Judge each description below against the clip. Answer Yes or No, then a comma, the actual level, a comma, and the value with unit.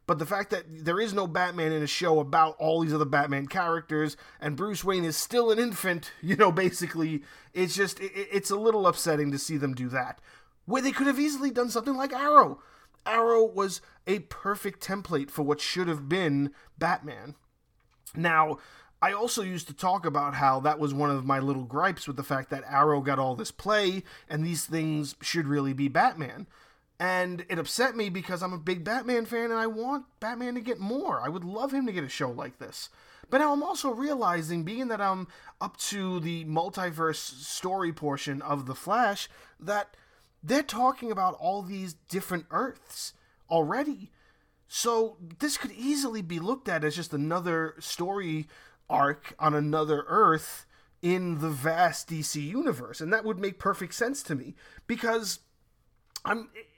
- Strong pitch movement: Yes, wide, 6.1 semitones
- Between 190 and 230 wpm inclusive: No, average, 180 wpm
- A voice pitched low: No, medium, 180 Hz